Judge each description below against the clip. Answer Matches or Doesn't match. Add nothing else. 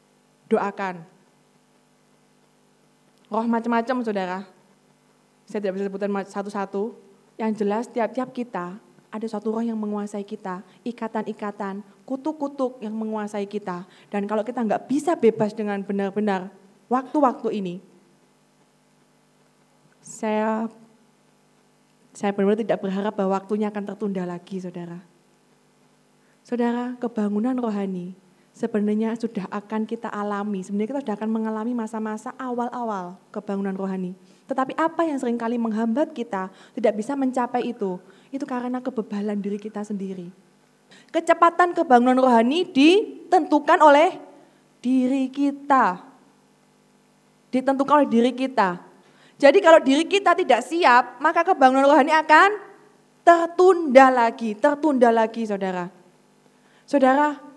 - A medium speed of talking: Matches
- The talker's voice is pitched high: Matches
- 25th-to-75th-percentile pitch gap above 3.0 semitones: Matches